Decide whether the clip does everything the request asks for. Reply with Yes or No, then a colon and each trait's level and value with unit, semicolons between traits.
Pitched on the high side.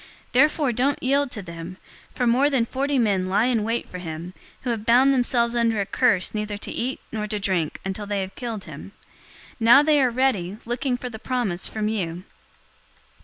Yes: high, 230 Hz